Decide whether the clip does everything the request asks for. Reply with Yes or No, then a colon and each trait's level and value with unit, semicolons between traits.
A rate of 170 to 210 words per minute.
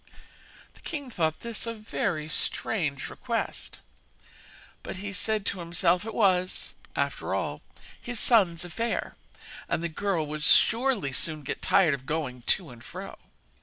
No: average, 140 wpm